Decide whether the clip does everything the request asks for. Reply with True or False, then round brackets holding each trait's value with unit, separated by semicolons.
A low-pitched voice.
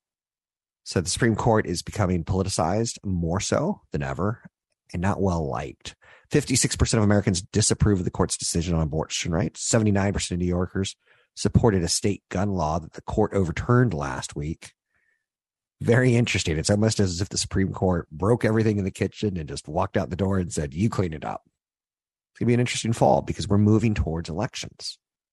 True (100 Hz)